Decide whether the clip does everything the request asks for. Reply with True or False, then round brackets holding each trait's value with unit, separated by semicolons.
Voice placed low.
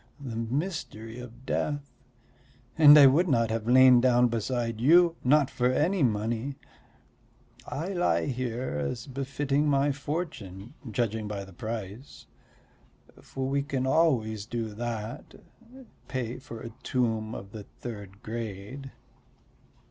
True (125 Hz)